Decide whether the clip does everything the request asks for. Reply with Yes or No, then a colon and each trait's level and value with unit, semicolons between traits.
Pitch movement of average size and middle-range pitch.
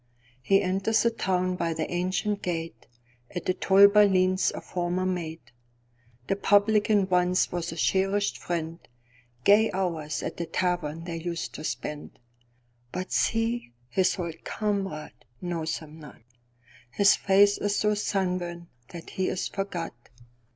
Yes: average, 4.7 semitones; medium, 175 Hz